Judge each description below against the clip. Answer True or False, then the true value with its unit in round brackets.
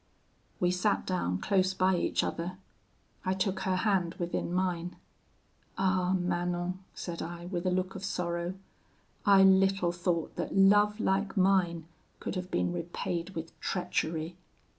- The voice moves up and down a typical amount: False (1.6 semitones)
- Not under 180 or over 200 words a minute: False (140 wpm)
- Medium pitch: True (180 Hz)